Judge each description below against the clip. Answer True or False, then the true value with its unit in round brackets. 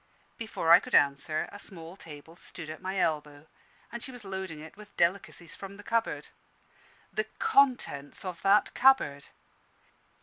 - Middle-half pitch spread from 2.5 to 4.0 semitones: False (5.3 semitones)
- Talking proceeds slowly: False (155 wpm)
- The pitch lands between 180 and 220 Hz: True (185 Hz)